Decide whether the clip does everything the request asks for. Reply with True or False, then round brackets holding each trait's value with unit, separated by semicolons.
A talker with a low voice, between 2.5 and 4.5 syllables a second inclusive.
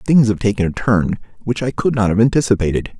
False (110 Hz; 5.9 syllables/s)